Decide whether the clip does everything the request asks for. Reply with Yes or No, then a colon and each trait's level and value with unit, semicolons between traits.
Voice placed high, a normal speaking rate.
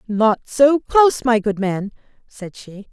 Yes: high, 230 Hz; average, 165 wpm